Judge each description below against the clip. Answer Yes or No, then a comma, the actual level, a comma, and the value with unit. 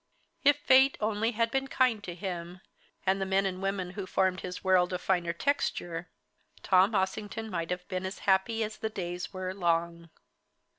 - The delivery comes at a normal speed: Yes, average, 180 wpm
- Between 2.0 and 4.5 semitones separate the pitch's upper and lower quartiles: Yes, average, 3.2 semitones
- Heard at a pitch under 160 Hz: No, high, 190 Hz